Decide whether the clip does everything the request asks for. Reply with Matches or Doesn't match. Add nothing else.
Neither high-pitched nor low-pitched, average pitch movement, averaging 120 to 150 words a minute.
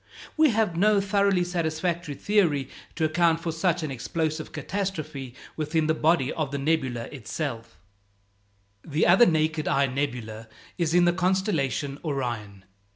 Matches